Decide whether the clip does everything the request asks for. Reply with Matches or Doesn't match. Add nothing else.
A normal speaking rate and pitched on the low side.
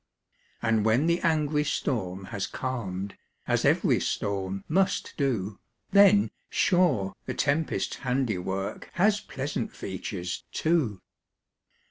Doesn't match